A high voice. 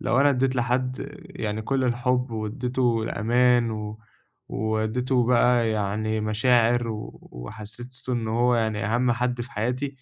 No: low, 120 Hz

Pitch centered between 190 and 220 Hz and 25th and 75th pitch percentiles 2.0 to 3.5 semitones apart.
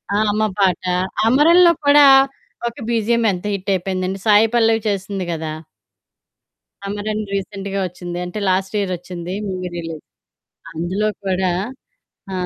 Yes: high, 195 Hz; average, 2.8 semitones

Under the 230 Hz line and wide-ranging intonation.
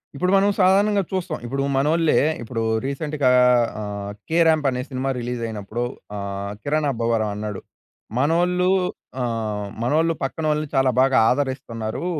Yes: low, 135 Hz; wide, 5.9 semitones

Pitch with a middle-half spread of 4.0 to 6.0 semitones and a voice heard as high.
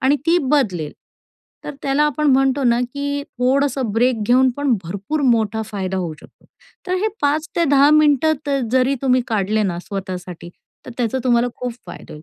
Yes: average, 5.1 semitones; very high, 255 Hz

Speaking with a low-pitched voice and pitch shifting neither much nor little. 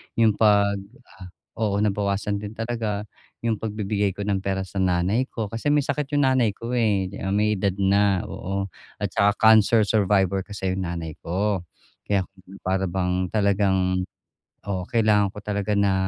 No: low, 100 Hz; narrow, 2.0 semitones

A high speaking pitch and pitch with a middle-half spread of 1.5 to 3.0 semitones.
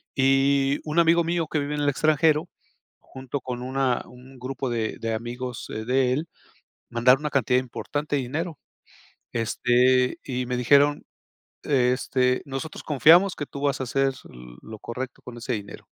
No: low, 135 Hz; average, 2.7 semitones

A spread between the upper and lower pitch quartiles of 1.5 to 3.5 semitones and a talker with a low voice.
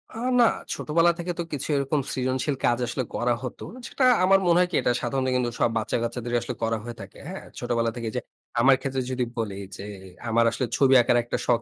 Yes: narrow, 2.6 semitones; low, 125 Hz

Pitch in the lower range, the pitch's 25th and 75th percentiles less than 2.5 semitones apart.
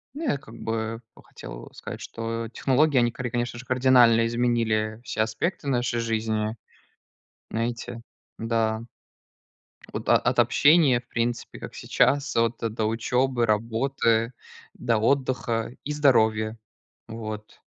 Yes: low, 115 Hz; narrow, 2.0 semitones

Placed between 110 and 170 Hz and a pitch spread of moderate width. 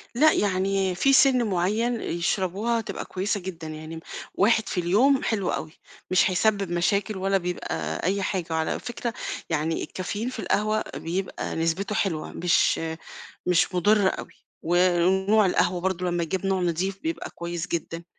No: high, 190 Hz; average, 3.2 semitones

